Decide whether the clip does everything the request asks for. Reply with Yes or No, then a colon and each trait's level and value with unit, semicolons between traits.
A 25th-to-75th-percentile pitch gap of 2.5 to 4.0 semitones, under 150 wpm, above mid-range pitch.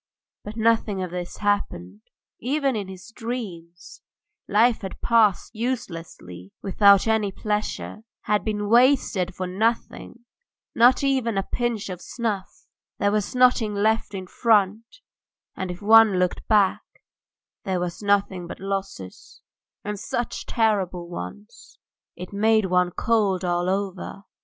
Yes: average, 3.5 semitones; slow, 135 wpm; high, 205 Hz